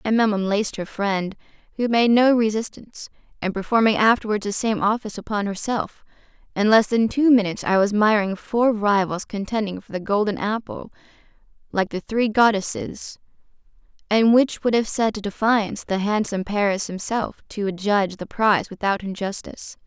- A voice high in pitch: Yes, high, 210 Hz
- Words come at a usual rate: Yes, average, 160 wpm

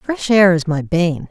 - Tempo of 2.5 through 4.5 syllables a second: Yes, 3.9 syllables/s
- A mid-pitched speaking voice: Yes, medium, 180 Hz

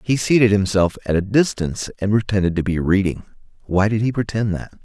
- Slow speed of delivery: No, average, 200 wpm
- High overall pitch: No, low, 100 Hz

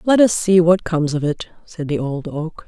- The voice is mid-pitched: Yes, medium, 170 Hz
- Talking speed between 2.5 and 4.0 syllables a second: No, 5.0 syllables/s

